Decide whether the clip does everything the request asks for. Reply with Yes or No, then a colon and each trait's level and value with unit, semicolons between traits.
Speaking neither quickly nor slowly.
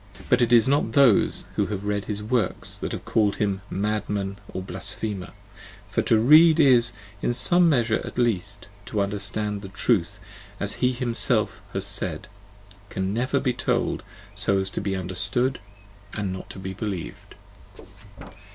Yes: average, 155 wpm